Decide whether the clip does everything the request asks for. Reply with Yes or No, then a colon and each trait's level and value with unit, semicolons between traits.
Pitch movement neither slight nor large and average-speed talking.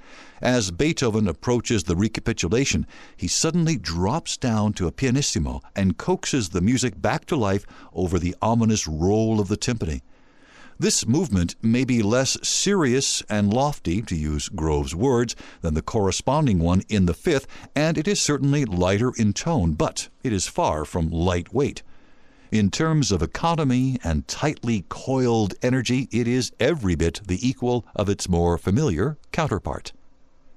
No: wide, 5.9 semitones; average, 150 wpm